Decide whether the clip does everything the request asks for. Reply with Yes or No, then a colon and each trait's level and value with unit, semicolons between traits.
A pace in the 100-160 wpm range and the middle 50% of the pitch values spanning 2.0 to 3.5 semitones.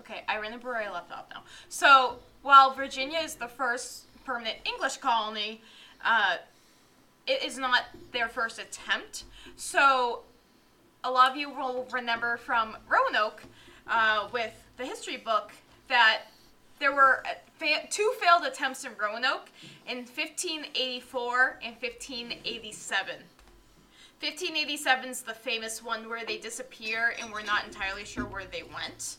Yes: average, 140 wpm; average, 3.1 semitones